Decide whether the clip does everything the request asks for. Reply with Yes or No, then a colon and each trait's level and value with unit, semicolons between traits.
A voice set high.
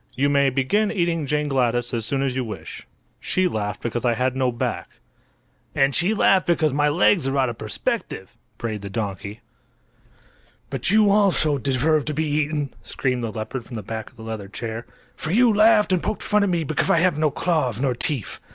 No: medium, 140 Hz